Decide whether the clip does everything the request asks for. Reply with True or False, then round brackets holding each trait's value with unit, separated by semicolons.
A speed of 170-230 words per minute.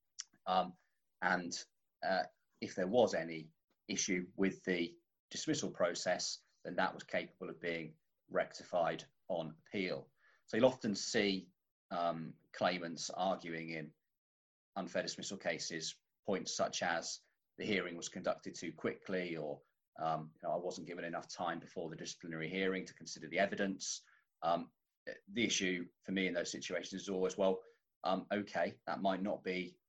False (150 wpm)